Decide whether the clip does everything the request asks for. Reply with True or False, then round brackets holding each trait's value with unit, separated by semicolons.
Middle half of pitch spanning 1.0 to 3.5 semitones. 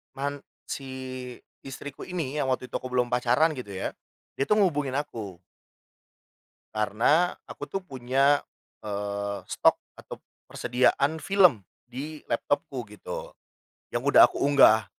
False (3.9 semitones)